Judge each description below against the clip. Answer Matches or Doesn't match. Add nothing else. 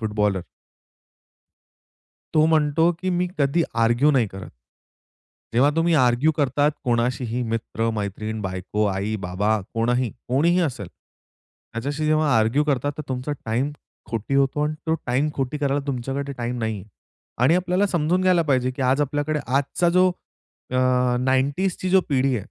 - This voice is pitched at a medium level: Doesn't match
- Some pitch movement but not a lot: Matches